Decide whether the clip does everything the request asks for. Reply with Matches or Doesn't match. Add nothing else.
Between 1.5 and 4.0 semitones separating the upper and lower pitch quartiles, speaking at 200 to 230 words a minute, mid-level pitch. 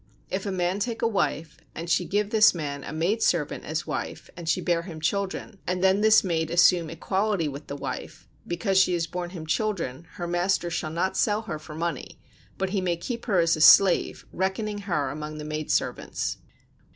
Matches